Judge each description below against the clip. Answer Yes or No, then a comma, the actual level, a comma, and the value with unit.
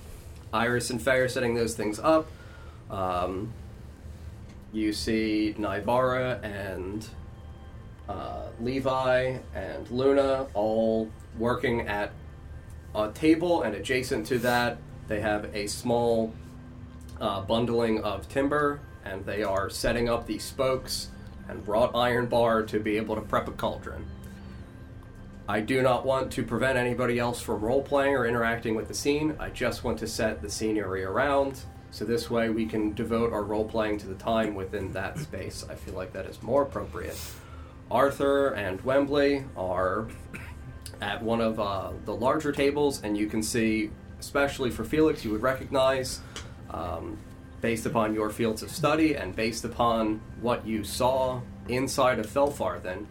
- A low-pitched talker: Yes, low, 110 Hz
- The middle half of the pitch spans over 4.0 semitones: No, average, 3.4 semitones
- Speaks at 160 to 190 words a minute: No, average, 150 wpm